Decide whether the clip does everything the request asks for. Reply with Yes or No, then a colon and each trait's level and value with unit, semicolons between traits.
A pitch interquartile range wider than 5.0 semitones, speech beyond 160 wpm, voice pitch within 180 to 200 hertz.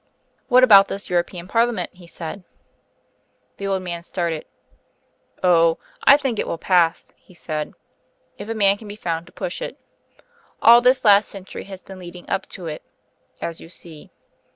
No: average, 3.3 semitones; average, 170 wpm; medium, 185 Hz